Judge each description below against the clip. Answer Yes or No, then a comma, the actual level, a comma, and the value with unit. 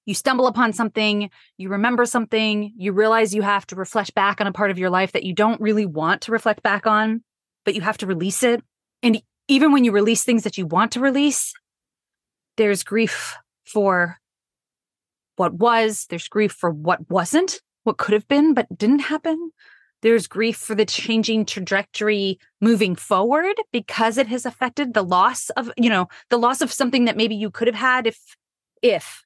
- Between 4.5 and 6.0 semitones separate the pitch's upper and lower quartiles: No, average, 3.2 semitones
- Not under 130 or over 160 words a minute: No, average, 190 wpm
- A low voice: No, high, 220 Hz